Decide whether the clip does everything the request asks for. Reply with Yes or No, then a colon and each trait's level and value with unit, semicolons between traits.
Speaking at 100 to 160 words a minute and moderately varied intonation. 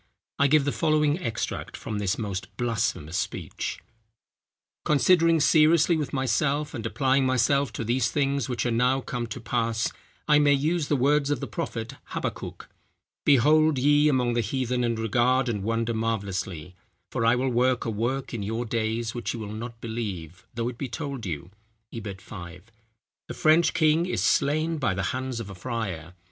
No: average, 175 wpm; average, 4.2 semitones